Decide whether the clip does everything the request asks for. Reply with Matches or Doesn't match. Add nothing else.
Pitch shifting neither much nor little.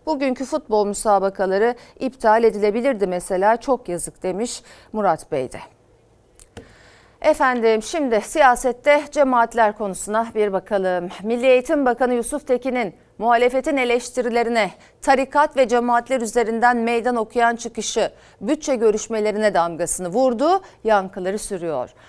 Matches